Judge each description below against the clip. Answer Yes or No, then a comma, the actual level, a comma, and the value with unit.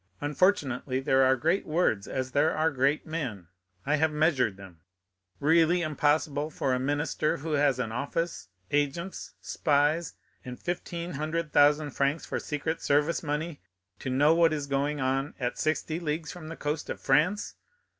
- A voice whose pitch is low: No, medium, 150 Hz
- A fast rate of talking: No, average, 160 wpm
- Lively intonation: No, average, 2.8 semitones